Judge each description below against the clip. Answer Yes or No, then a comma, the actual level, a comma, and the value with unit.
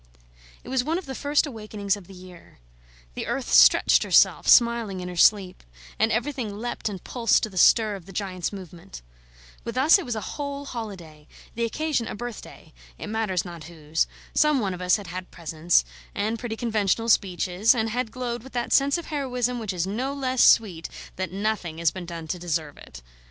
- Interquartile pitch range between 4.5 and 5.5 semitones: Yes, average, 5.2 semitones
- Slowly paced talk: No, average, 200 wpm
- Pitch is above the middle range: Yes, high, 210 Hz